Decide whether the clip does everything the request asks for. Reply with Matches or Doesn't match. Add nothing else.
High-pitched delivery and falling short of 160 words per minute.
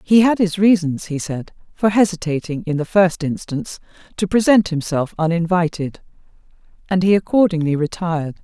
Doesn't match